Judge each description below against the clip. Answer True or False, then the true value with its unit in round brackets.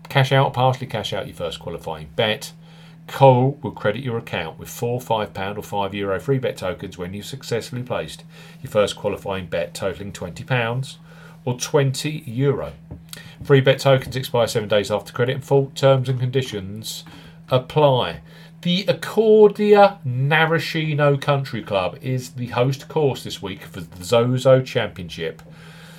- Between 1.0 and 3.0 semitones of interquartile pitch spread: False (5.2 semitones)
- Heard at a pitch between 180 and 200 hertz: False (135 Hz)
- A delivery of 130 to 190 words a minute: True (155 wpm)